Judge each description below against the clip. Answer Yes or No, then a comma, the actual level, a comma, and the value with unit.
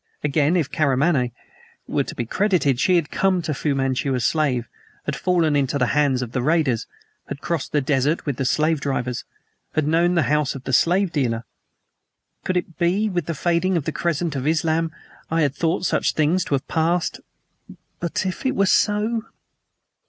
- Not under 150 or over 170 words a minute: No, average, 190 wpm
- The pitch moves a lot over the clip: No, average, 4.0 semitones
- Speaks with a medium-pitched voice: Yes, medium, 155 Hz